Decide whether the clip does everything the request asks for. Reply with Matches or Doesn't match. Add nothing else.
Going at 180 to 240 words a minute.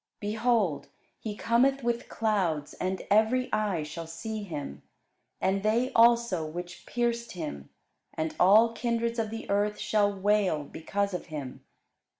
Doesn't match